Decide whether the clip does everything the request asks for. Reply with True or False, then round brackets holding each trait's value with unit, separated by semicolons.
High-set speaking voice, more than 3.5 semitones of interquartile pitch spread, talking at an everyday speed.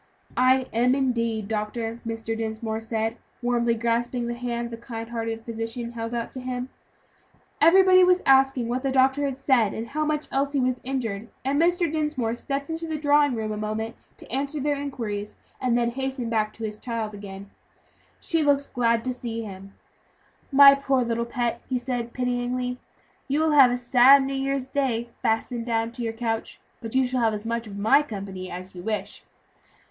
False (240 Hz; 3.1 semitones; 190 wpm)